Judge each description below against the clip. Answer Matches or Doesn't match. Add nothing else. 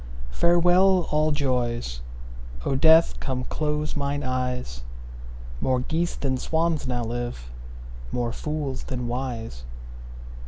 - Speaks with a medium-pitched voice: Doesn't match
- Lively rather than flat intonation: Doesn't match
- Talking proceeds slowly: Matches